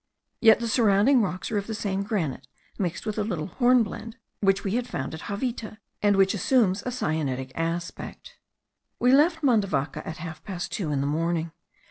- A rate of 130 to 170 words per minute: No, average, 180 wpm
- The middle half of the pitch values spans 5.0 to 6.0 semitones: Yes, wide, 5.5 semitones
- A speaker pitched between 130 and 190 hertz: No, high, 200 Hz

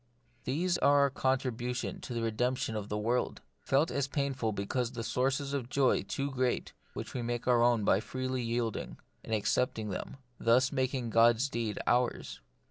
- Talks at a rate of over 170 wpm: Yes, average, 180 wpm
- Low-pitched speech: Yes, low, 125 Hz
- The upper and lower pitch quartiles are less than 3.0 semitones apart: Yes, narrow, 2.5 semitones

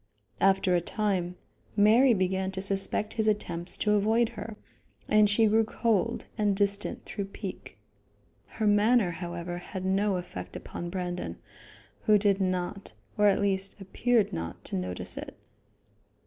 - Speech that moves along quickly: No, average, 145 wpm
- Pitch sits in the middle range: No, high, 195 Hz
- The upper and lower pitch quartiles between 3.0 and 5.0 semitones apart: No, narrow, 2.6 semitones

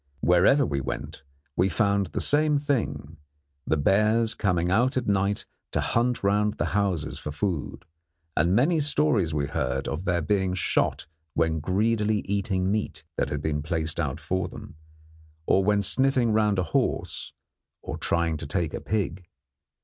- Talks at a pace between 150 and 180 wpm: Yes, average, 160 wpm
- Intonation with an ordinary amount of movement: Yes, average, 4.4 semitones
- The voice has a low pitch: Yes, very low, 95 Hz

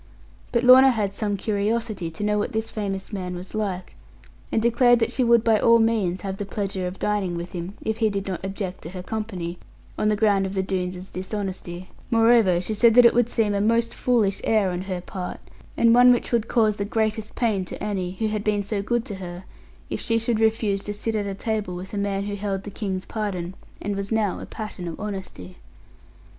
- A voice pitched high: Yes, high, 205 Hz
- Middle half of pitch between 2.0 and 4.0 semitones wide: Yes, average, 2.8 semitones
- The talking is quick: Yes, fast, 220 wpm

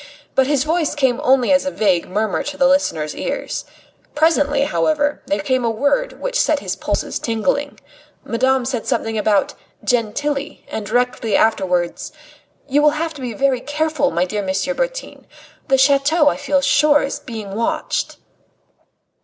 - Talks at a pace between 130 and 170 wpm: Yes, average, 160 wpm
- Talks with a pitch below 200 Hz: No, very high, 270 Hz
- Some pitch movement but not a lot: Yes, average, 4.6 semitones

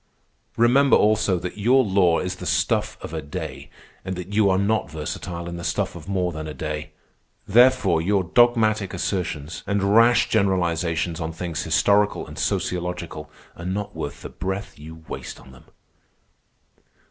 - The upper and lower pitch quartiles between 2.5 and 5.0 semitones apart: Yes, average, 3.8 semitones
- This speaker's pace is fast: No, average, 160 wpm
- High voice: No, very low, 90 Hz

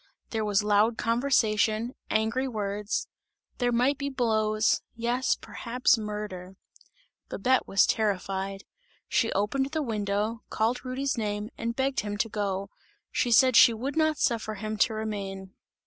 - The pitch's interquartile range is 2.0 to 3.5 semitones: Yes, average, 3.0 semitones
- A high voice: Yes, high, 220 Hz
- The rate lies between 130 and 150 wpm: Yes, average, 140 wpm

